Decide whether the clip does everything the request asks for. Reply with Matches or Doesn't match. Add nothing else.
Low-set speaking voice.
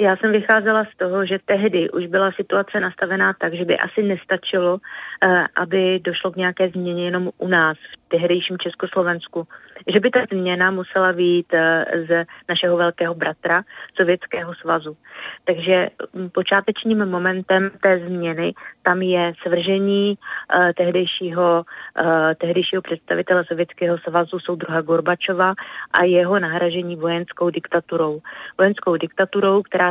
Doesn't match